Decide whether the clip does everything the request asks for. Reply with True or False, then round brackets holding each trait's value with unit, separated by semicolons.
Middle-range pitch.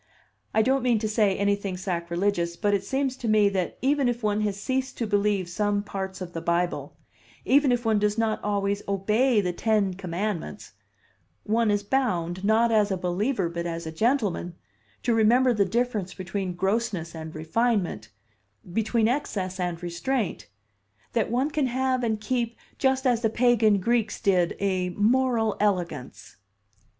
False (205 Hz)